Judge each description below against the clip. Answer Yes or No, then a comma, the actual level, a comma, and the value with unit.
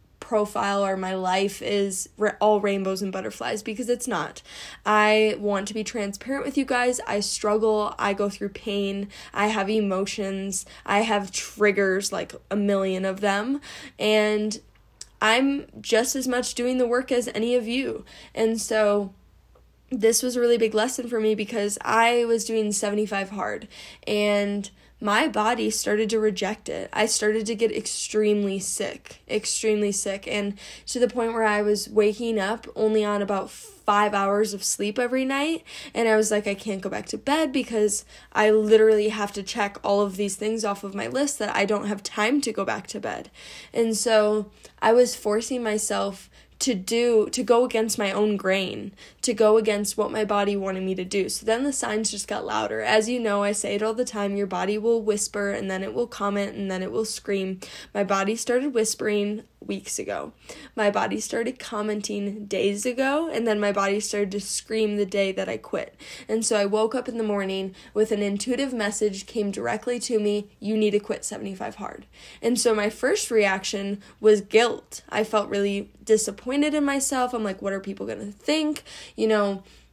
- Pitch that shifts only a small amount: Yes, narrow, 2.1 semitones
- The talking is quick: No, average, 190 wpm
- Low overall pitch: No, high, 210 Hz